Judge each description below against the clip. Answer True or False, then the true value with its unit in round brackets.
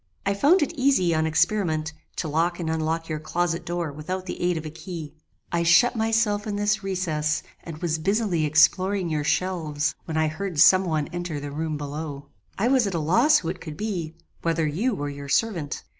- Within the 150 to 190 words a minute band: False (205 wpm)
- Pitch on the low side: False (170 Hz)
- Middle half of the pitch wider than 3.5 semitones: True (4.0 semitones)